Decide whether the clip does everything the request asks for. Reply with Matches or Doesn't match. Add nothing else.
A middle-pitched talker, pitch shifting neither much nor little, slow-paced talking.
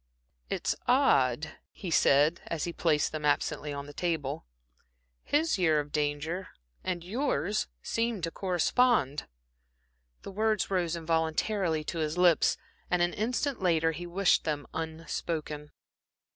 Matches